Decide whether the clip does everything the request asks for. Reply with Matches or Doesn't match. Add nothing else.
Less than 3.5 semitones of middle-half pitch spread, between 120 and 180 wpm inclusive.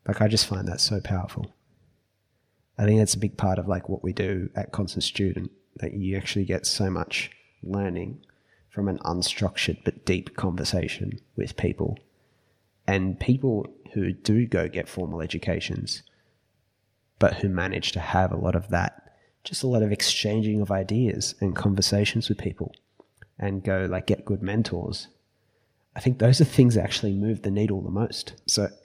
Matches